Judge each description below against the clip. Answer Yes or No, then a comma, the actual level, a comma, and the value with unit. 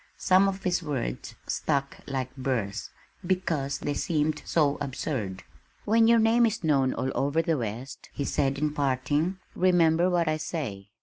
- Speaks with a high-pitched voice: No, medium, 150 Hz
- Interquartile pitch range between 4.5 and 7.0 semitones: Yes, average, 4.9 semitones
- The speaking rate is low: No, average, 160 wpm